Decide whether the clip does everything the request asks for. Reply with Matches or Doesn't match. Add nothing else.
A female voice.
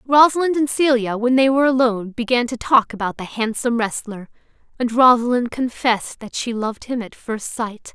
Matches